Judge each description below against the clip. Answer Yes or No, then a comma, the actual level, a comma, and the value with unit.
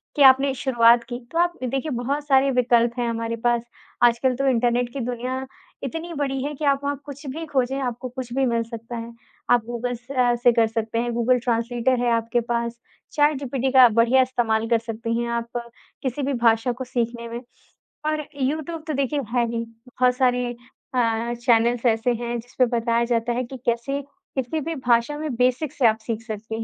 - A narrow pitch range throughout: Yes, narrow, 2.3 semitones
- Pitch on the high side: Yes, high, 245 Hz